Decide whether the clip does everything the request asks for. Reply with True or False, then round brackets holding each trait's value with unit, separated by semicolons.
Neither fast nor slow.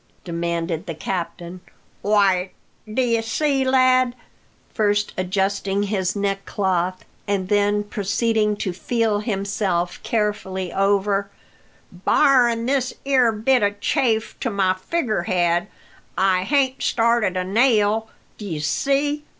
False (110 wpm)